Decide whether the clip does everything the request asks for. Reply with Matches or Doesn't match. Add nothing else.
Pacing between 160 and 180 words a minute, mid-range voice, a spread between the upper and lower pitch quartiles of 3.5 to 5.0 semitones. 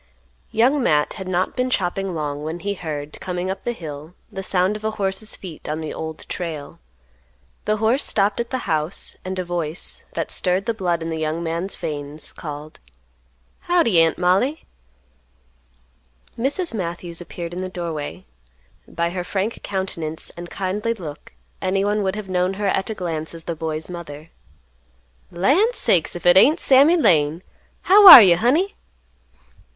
Matches